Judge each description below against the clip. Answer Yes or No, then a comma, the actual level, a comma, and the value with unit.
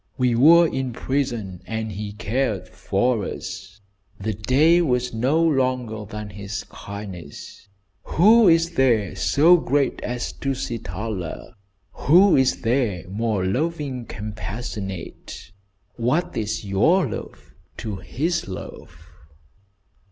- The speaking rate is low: Yes, slow, 110 wpm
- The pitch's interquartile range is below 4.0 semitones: No, wide, 5.4 semitones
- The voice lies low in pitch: Yes, low, 115 Hz